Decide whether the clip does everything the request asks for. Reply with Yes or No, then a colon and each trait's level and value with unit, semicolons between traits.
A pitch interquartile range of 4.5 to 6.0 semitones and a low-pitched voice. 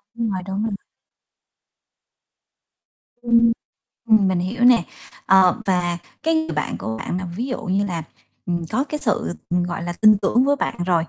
No: average, 4.8 semitones; high, 195 Hz